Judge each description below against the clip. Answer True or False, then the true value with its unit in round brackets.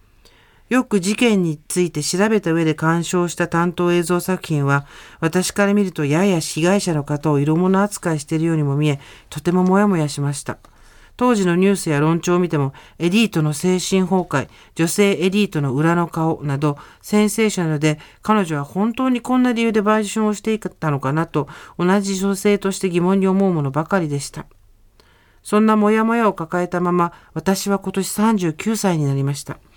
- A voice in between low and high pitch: True (175 Hz)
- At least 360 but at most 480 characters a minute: False (345 characters per minute)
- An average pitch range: True (4.4 semitones)